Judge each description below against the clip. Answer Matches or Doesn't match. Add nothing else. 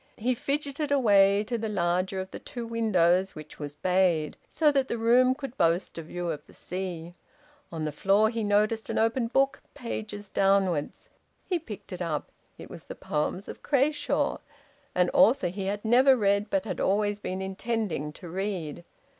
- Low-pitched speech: Doesn't match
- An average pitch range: Matches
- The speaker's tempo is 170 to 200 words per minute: Matches